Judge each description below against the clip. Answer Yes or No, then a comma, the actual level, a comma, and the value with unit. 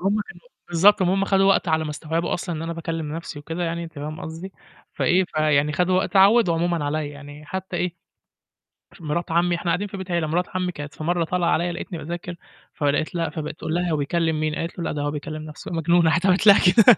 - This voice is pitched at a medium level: Yes, medium, 170 Hz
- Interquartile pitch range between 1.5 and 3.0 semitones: Yes, narrow, 2.6 semitones